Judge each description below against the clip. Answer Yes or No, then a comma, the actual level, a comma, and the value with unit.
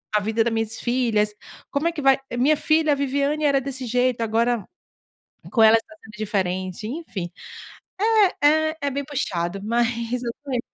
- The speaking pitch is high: Yes, high, 240 Hz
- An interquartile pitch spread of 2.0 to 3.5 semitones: No, average, 4.3 semitones